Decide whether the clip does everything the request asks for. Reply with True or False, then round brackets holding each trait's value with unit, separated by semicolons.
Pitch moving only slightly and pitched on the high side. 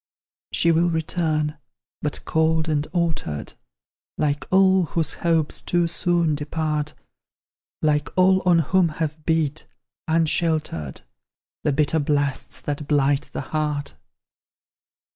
False (2.2 semitones; 155 Hz)